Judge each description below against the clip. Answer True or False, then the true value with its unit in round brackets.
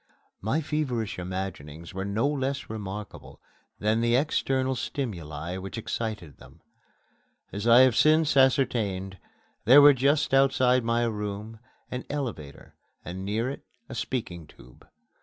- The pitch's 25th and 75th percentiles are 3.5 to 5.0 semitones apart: False (5.5 semitones)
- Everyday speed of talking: False (130 wpm)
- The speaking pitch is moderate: False (115 Hz)